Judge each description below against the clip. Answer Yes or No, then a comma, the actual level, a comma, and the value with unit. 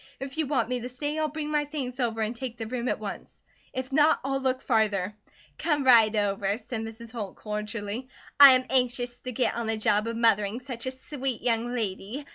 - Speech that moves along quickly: Yes, fast, 215 wpm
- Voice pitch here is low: No, high, 245 Hz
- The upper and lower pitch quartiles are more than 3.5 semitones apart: No, average, 3.1 semitones